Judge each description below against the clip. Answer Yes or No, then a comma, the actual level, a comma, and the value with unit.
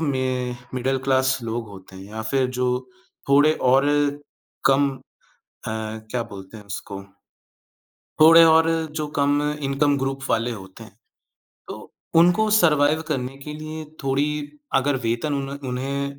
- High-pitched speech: No, low, 135 Hz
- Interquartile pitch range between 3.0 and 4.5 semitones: Yes, average, 3.6 semitones